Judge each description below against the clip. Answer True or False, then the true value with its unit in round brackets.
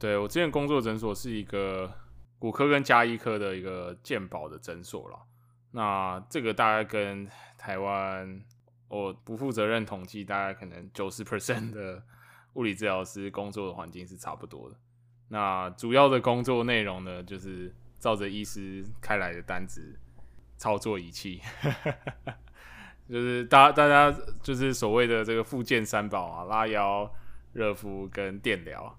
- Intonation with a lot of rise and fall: False (3.9 semitones)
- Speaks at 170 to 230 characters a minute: False (245 characters per minute)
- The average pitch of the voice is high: False (105 Hz)